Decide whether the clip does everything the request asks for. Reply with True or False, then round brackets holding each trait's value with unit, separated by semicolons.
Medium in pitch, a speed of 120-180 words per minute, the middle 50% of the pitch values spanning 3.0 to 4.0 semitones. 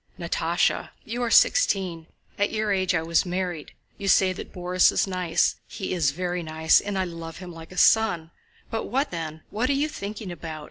False (180 Hz; 190 wpm; 3.5 semitones)